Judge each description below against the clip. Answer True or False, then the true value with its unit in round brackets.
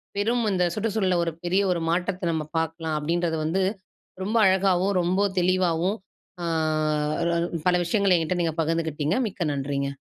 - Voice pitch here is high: False (175 Hz)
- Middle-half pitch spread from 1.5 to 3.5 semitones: True (2.8 semitones)